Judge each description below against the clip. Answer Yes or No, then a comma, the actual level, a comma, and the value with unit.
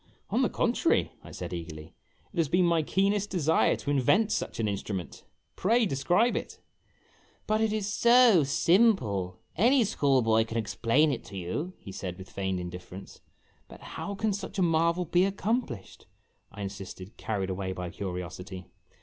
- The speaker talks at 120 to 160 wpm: No, average, 175 wpm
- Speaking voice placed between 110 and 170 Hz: Yes, medium, 140 Hz